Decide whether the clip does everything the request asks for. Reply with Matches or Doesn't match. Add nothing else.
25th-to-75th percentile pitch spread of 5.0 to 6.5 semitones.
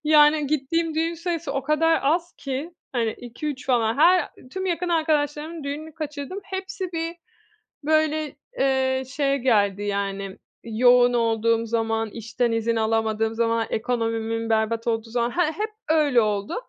Matches